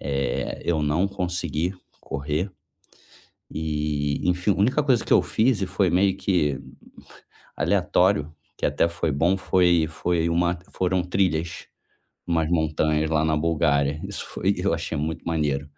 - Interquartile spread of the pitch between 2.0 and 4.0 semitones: Yes, average, 3.0 semitones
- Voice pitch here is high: No, very low, 85 Hz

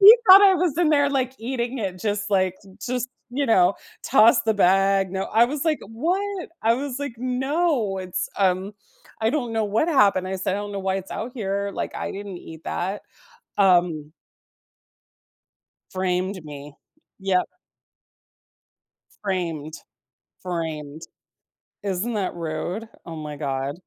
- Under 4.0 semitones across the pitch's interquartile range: No, wide, 5.4 semitones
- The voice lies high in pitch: Yes, high, 200 Hz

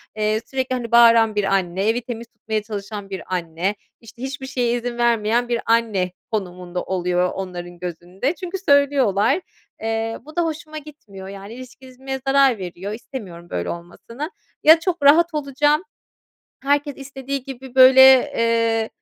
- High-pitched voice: Yes, high, 230 Hz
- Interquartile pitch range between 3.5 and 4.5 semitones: No, wide, 5.4 semitones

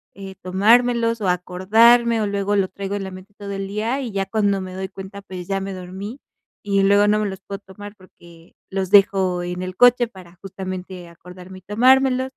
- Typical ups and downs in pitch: No, narrow, 2.2 semitones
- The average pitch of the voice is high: Yes, high, 195 Hz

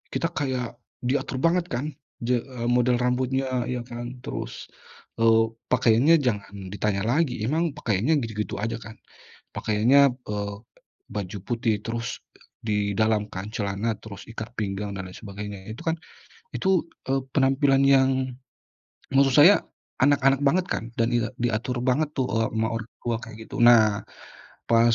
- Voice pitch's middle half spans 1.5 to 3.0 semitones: No, average, 3.7 semitones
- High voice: No, low, 120 Hz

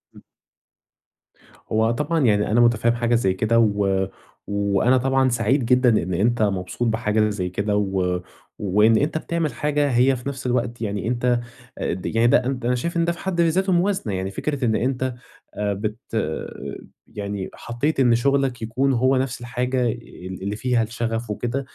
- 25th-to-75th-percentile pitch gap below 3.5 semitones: No, average, 4.0 semitones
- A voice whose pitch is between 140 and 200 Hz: No, low, 120 Hz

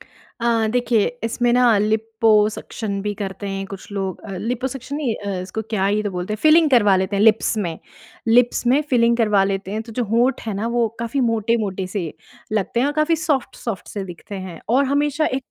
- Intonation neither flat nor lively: Yes, average, 3.5 semitones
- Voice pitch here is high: Yes, high, 220 Hz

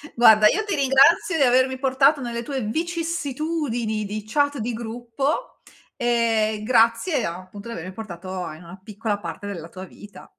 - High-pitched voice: Yes, high, 235 Hz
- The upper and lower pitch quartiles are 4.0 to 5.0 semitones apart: Yes, average, 4.5 semitones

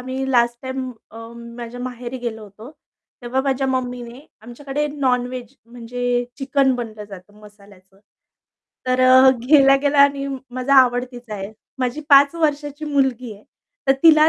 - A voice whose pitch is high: Yes, very high, 255 Hz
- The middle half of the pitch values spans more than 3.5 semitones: No, narrow, 2.5 semitones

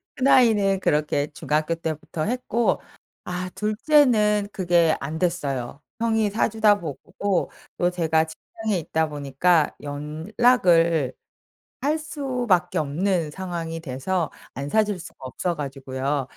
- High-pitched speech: No, medium, 175 Hz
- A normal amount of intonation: No, wide, 5.7 semitones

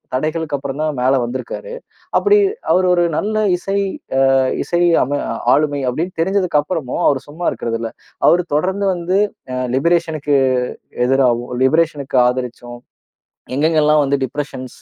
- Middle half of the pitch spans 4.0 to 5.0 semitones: Yes, average, 4.7 semitones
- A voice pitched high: No, medium, 150 Hz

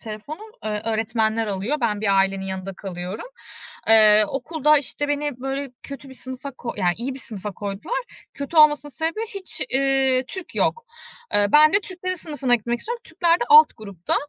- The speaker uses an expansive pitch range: Yes, wide, 6.3 semitones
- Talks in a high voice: Yes, very high, 260 Hz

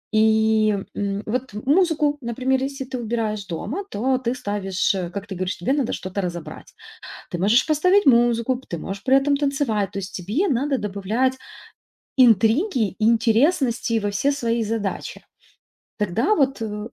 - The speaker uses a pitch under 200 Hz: No, high, 230 Hz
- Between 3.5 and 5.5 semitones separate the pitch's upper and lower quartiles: Yes, average, 4.6 semitones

